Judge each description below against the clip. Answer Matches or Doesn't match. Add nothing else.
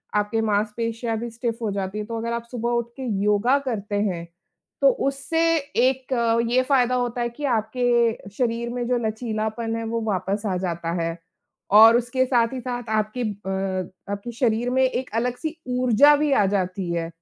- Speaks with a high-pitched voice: Matches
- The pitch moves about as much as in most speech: Matches